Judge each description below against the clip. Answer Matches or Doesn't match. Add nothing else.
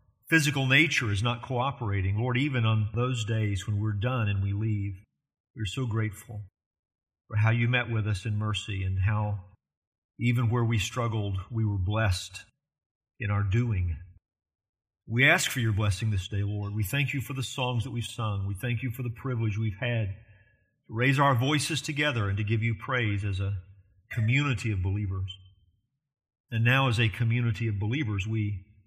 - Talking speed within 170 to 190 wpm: Matches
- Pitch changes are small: Doesn't match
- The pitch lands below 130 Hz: Matches